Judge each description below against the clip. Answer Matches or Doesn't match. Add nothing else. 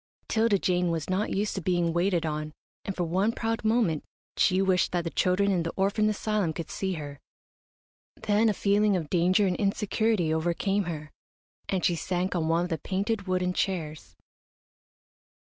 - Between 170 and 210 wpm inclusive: Matches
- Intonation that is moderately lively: Matches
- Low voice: Doesn't match